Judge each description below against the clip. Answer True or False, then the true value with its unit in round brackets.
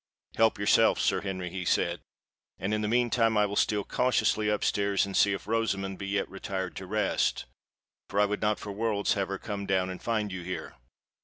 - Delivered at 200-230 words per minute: True (205 wpm)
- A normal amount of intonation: False (1.8 semitones)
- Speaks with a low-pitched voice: True (100 Hz)